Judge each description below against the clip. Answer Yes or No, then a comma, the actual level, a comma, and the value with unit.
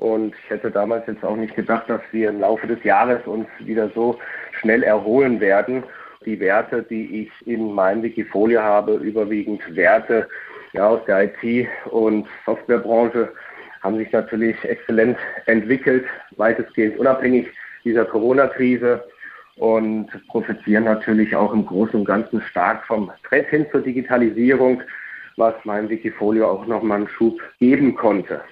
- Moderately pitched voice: No, low, 110 Hz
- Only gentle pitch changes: Yes, narrow, 1.7 semitones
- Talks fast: No, average, 145 wpm